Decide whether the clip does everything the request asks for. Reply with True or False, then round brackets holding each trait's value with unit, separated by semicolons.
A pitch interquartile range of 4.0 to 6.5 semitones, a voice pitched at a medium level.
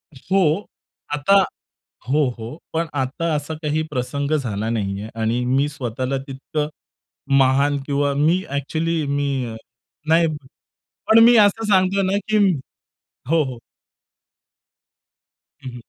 True (4.4 semitones; 145 Hz)